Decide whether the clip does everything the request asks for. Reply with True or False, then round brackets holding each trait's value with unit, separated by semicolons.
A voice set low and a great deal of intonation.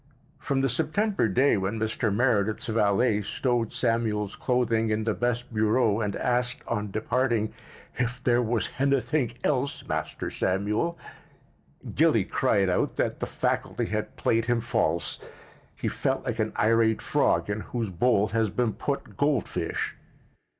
False (115 Hz; 2.7 semitones)